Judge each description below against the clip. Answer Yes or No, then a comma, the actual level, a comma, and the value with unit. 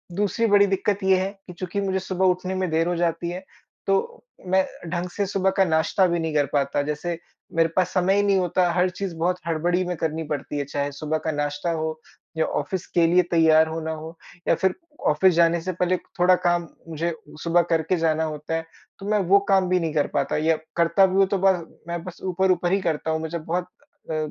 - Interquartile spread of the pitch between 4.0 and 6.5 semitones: No, average, 2.7 semitones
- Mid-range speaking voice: Yes, medium, 175 Hz